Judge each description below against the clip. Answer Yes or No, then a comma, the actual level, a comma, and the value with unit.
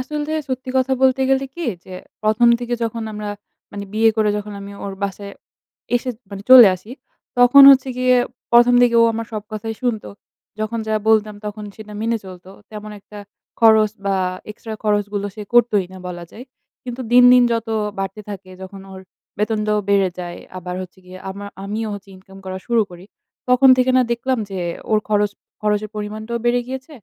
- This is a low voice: No, high, 215 Hz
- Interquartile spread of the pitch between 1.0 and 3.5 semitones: Yes, average, 3.1 semitones